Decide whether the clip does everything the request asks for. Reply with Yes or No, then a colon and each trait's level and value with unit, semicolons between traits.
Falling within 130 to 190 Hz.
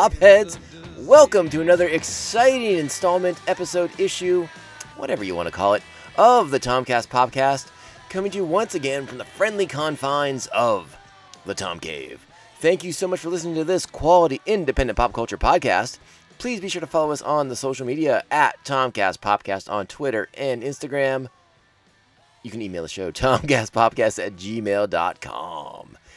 Yes: medium, 140 Hz